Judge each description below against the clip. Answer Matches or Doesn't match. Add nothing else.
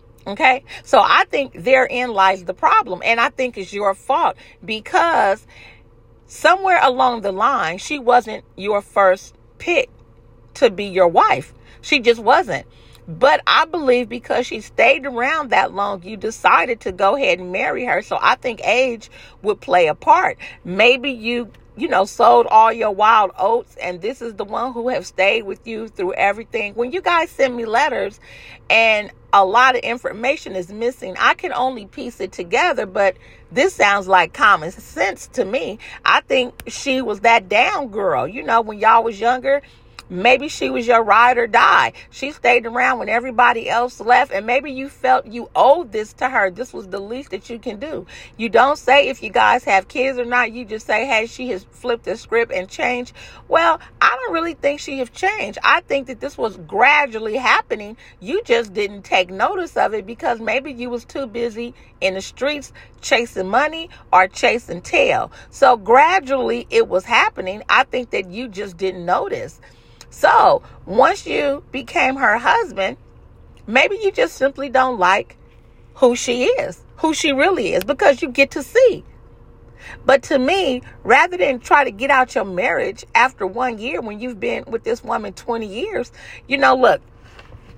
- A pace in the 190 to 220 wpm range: Doesn't match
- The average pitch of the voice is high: Matches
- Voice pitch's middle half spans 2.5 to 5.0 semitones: Matches